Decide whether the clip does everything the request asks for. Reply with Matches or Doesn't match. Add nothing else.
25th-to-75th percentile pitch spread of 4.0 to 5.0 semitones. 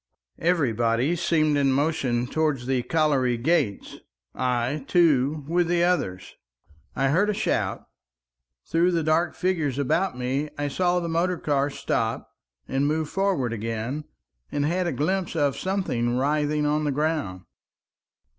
Matches